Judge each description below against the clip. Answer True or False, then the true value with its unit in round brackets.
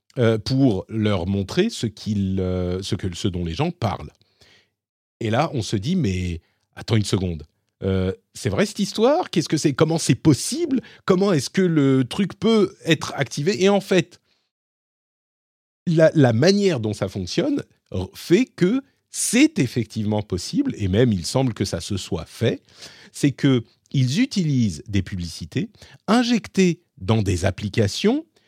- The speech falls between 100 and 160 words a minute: True (145 wpm)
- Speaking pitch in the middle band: False (120 Hz)